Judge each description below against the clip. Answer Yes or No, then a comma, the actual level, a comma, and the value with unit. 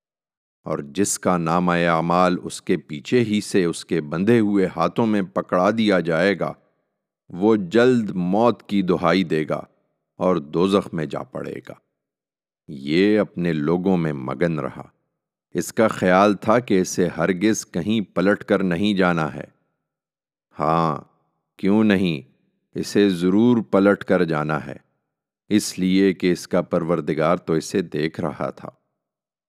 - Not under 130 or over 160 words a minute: Yes, average, 145 wpm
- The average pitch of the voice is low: Yes, very low, 90 Hz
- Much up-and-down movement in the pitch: No, average, 4.0 semitones